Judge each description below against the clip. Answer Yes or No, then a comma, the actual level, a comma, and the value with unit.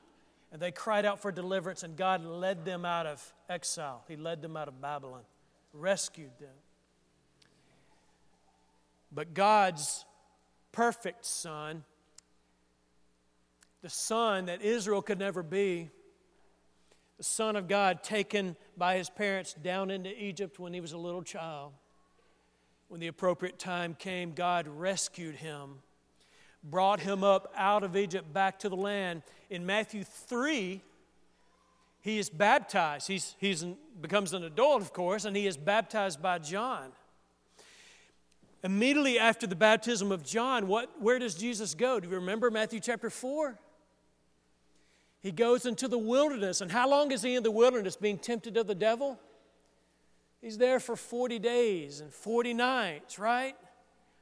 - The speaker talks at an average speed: Yes, average, 145 wpm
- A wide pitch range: Yes, wide, 5.7 semitones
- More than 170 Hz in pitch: Yes, high, 190 Hz